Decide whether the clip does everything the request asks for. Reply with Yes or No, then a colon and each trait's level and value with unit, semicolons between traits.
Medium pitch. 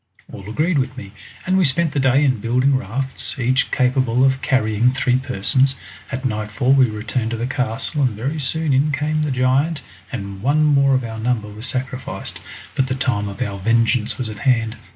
No: low, 130 Hz